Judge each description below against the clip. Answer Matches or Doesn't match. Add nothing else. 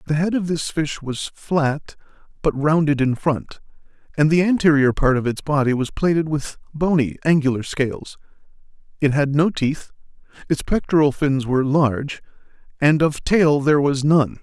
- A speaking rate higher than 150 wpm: Matches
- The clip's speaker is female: Doesn't match